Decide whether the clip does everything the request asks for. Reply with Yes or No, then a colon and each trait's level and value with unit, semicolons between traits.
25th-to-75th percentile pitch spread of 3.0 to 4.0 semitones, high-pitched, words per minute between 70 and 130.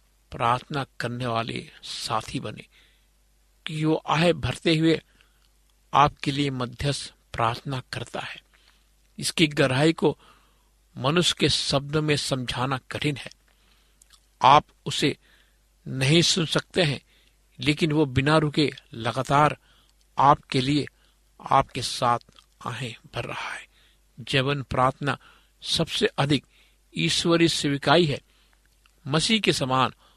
No: average, 3.7 semitones; medium, 140 Hz; slow, 110 wpm